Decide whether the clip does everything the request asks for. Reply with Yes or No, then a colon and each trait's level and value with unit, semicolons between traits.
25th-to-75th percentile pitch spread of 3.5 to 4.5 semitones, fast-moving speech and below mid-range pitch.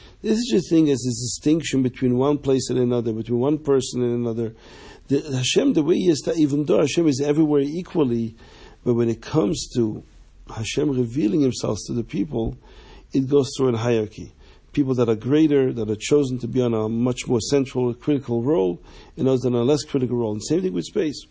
Yes: average, 3.8 semitones; fast, 210 wpm; low, 125 Hz